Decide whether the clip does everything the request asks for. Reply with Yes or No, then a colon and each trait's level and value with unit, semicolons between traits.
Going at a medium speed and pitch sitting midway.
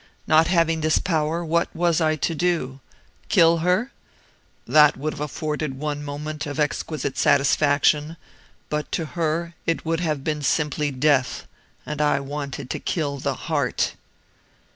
Yes: average, 145 wpm; medium, 155 Hz